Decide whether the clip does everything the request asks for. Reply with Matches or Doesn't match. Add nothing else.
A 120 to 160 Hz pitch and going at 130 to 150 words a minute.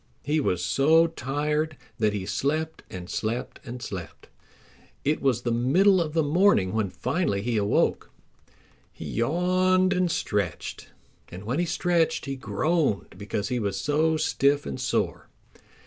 Matches